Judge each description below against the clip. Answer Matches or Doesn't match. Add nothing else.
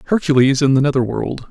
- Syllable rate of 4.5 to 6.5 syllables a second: Matches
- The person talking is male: Matches